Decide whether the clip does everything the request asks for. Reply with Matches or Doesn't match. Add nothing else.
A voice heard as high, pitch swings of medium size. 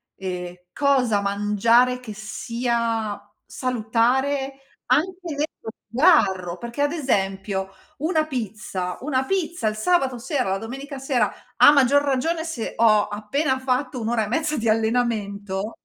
Matches